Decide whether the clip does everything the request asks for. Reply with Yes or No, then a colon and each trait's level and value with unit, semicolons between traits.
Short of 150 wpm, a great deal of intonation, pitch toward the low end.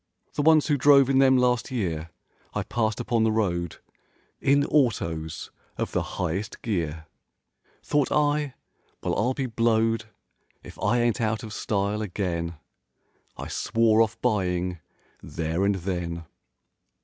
Yes: slow, 135 wpm; wide, 5.8 semitones; low, 110 Hz